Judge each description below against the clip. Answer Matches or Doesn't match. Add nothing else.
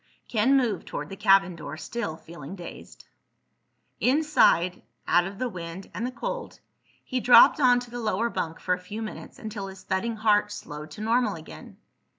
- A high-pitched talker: Matches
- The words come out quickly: Doesn't match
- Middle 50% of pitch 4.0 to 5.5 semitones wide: Matches